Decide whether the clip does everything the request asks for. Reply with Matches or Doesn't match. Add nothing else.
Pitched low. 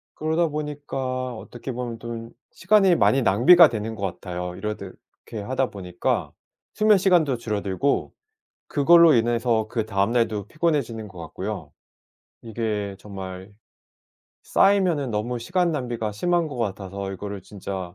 Matches